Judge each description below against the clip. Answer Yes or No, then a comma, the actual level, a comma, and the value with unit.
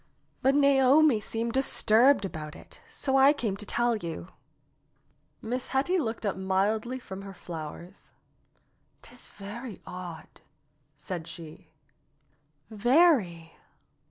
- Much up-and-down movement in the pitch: Yes, wide, 6.3 semitones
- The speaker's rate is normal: No, slow, 110 wpm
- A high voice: Yes, high, 220 Hz